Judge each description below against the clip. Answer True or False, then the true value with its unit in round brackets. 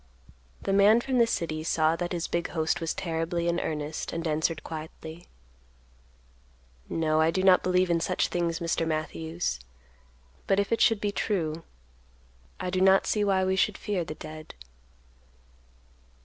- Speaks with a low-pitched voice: False (170 Hz)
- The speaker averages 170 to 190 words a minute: False (160 wpm)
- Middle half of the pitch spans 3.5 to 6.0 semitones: False (3.0 semitones)